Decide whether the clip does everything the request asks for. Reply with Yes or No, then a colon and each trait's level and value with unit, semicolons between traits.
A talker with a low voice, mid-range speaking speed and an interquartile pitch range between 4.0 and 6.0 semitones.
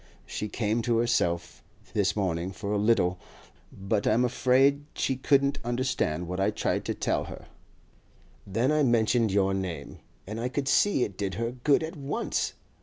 Yes: low, 115 Hz; average, 170 wpm; average, 5.0 semitones